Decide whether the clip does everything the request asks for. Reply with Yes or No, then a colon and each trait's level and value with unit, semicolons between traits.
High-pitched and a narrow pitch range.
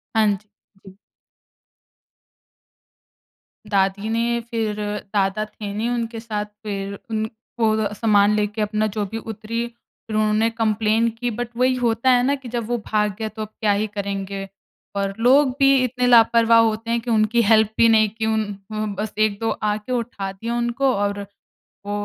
Yes: high, 220 Hz; narrow, 2.0 semitones